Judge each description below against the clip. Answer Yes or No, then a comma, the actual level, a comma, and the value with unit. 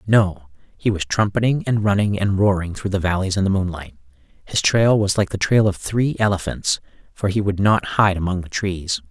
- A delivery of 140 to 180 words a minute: No, fast, 205 wpm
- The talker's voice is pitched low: Yes, very low, 95 Hz